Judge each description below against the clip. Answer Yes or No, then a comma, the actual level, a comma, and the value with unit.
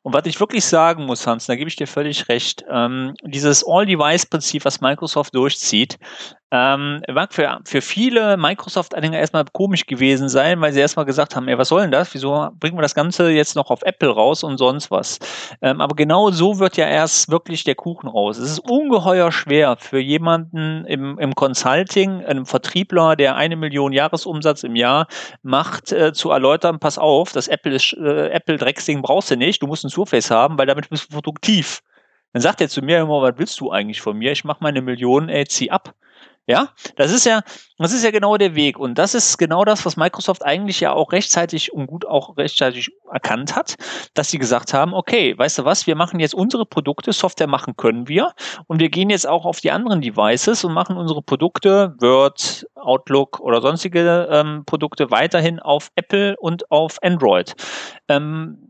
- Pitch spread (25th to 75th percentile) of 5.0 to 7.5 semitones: No, average, 4.0 semitones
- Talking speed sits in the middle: No, fast, 195 wpm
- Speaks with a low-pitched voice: No, medium, 155 Hz